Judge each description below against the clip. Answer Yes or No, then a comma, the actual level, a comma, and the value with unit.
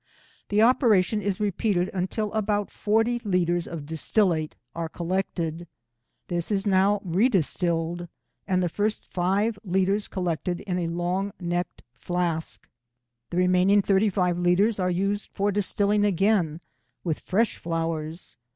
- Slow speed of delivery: Yes, slow, 130 wpm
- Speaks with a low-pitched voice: No, medium, 185 Hz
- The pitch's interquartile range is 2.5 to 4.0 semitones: Yes, average, 2.9 semitones